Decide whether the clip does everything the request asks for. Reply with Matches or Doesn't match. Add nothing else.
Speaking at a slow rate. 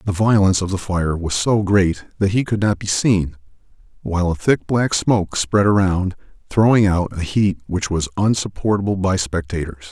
Doesn't match